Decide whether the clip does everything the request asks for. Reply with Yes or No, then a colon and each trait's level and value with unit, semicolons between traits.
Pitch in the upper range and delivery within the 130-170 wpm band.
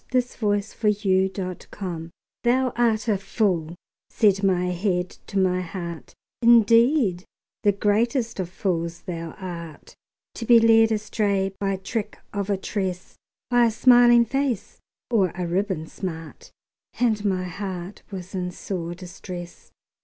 Yes: high, 195 Hz; slow, 135 wpm